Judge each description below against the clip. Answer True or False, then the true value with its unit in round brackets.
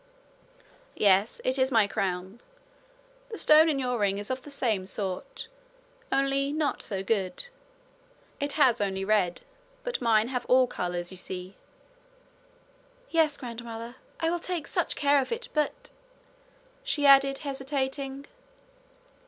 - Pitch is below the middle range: False (260 Hz)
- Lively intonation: True (5.8 semitones)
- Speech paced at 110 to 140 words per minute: True (135 wpm)